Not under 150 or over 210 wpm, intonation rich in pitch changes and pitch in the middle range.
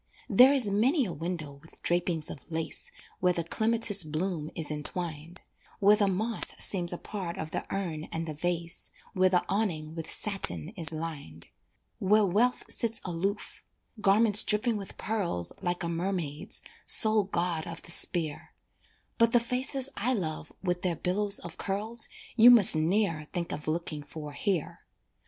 No: average, 160 wpm; average, 4.5 semitones; medium, 180 Hz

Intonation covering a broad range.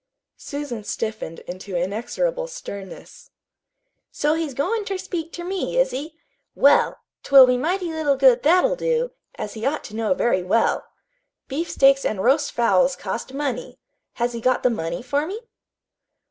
Yes: wide, 6.3 semitones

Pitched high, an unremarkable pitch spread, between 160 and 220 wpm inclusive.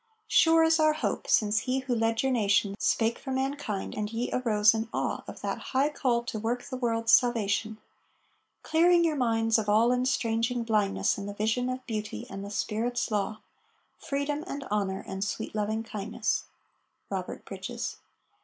Yes: high, 230 Hz; average, 3.3 semitones; average, 170 wpm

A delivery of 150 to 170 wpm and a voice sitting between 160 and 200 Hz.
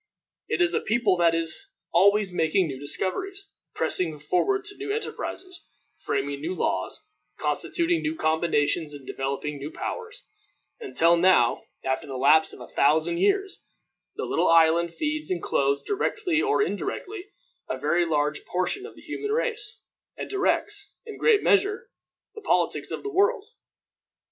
Yes: average, 155 wpm; medium, 185 Hz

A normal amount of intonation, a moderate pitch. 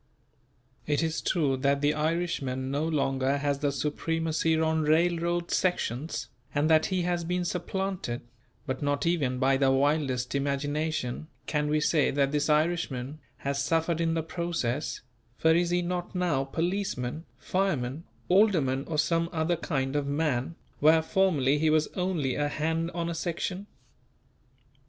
Yes: average, 3.4 semitones; medium, 155 Hz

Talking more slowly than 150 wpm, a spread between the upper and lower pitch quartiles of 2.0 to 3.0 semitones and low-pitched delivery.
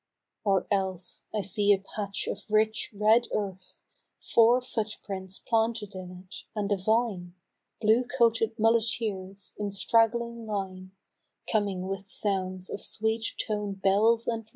No: average, 140 wpm; average, 2.7 semitones; high, 210 Hz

